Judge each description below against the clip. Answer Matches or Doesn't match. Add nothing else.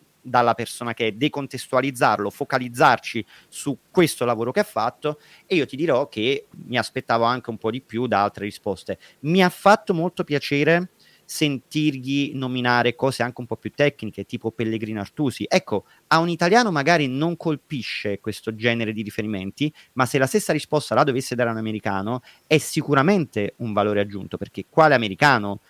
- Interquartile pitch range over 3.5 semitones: Matches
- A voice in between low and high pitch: Doesn't match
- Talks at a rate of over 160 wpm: Matches